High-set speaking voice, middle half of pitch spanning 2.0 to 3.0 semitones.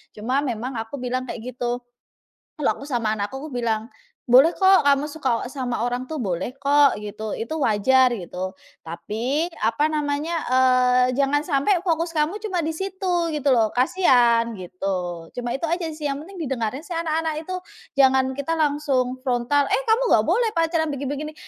No: very high, 270 Hz; average, 4.7 semitones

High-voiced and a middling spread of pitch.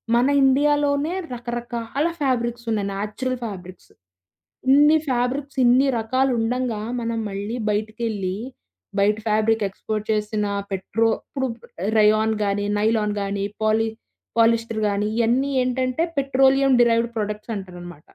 Yes: high, 225 Hz; average, 3.4 semitones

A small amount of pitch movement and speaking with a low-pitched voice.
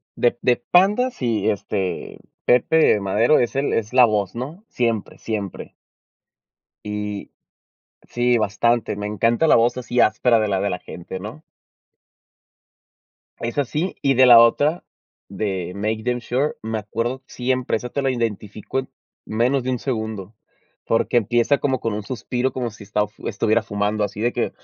No: average, 3.3 semitones; low, 115 Hz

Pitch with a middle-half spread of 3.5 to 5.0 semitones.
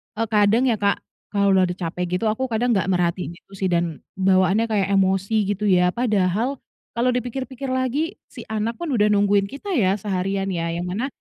Yes: average, 3.9 semitones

